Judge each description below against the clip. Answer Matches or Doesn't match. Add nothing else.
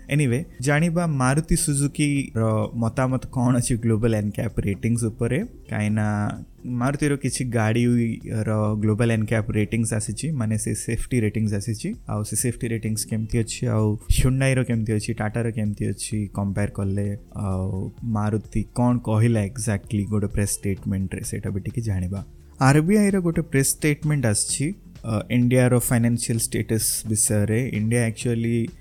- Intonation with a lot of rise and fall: Doesn't match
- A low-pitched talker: Matches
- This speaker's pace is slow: Doesn't match